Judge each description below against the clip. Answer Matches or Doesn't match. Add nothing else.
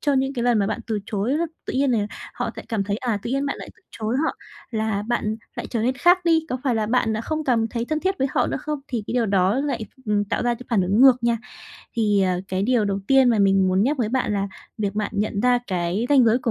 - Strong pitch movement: Doesn't match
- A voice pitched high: Matches